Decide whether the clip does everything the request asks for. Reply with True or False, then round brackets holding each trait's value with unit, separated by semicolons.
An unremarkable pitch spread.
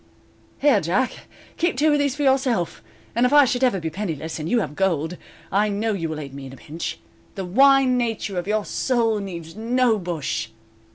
False (7.1 semitones)